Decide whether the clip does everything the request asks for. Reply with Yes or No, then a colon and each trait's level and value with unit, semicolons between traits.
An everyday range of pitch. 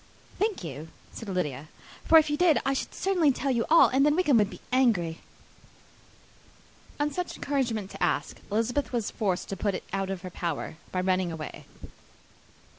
No: wide, 7.8 semitones